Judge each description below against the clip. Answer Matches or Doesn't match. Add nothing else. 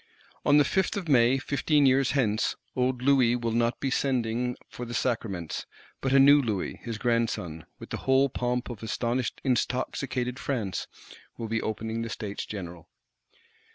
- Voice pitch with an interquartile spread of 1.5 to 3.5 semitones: Matches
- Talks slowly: Doesn't match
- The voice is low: Matches